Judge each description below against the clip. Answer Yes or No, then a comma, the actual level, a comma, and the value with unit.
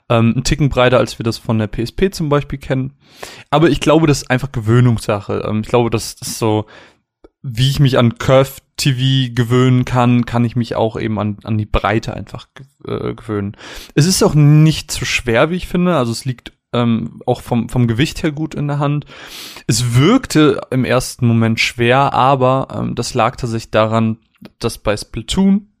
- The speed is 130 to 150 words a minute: No, average, 180 wpm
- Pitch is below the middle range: Yes, low, 125 Hz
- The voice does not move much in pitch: No, average, 3.6 semitones